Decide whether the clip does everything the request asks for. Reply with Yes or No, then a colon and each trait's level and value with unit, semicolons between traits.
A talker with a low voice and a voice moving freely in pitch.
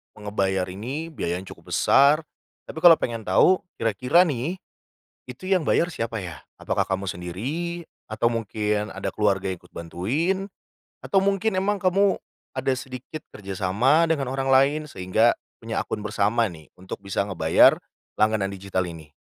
Yes: low, 115 Hz; wide, 8.1 semitones